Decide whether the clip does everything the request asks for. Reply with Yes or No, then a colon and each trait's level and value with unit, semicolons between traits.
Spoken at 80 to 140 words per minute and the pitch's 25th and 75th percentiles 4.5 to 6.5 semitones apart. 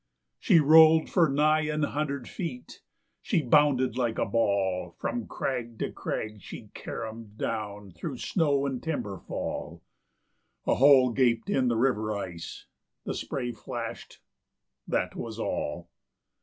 Yes: slow, 135 wpm; wide, 5.4 semitones